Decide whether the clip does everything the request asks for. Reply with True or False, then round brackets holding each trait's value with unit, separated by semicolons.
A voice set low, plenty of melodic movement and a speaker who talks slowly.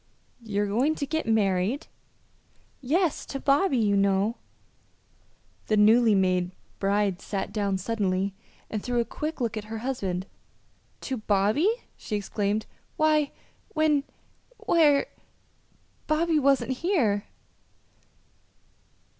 False (225 Hz; 6.0 semitones; 110 wpm)